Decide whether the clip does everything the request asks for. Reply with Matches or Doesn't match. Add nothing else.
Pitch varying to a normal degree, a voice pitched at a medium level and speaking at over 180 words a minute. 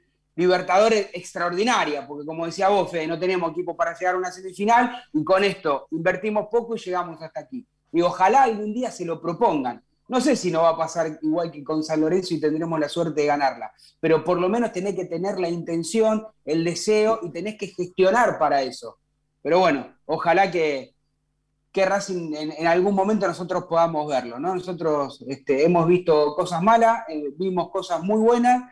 Matches